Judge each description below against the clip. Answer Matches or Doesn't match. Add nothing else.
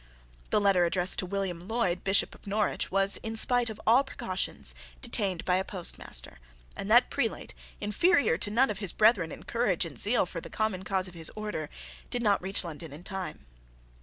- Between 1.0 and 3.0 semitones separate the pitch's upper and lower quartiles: Doesn't match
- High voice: Matches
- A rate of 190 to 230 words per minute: Matches